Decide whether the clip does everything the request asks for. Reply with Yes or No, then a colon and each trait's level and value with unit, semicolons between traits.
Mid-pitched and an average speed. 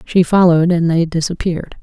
Yes: medium, 170 Hz; average, 165 wpm